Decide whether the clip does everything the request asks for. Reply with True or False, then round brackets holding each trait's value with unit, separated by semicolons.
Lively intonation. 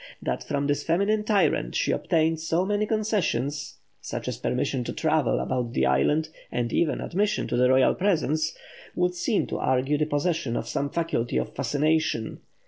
False (5.0 semitones)